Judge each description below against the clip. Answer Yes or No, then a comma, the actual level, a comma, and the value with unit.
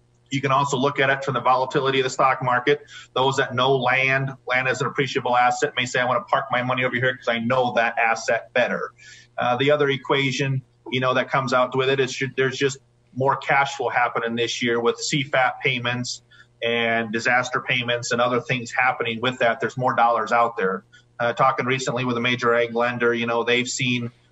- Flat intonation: Yes, narrow, 2.0 semitones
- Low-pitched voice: Yes, low, 125 Hz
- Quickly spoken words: Yes, fast, 215 wpm